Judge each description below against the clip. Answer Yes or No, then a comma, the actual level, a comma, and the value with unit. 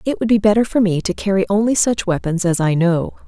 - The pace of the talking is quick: Yes, fast, 255 wpm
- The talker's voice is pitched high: Yes, high, 195 Hz